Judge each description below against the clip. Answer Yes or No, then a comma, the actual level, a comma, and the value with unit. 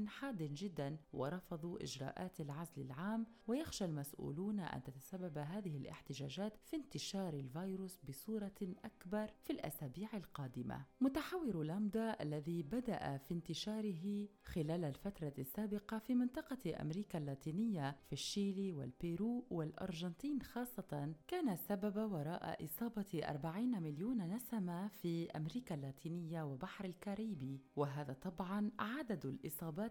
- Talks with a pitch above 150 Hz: Yes, medium, 185 Hz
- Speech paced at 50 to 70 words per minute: No, average, 110 wpm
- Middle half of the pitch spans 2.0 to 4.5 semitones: No, wide, 5.6 semitones